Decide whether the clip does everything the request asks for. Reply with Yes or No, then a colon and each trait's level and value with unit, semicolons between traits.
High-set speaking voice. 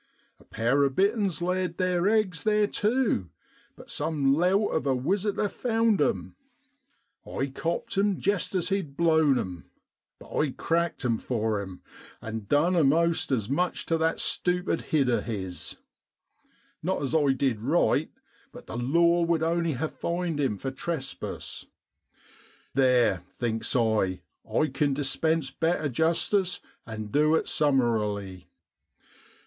No: medium, 155 Hz